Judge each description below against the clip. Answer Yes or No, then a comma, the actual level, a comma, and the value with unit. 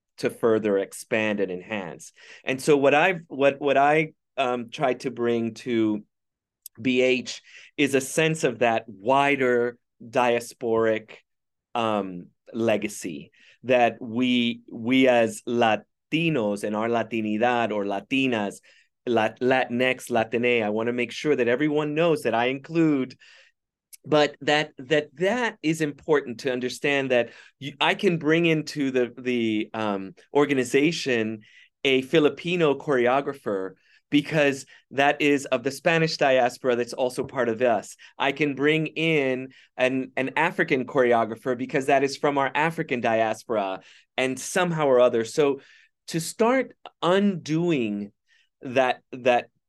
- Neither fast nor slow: No, slow, 130 wpm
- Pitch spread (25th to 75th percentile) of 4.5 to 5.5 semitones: No, average, 4.1 semitones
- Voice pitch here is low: Yes, low, 130 Hz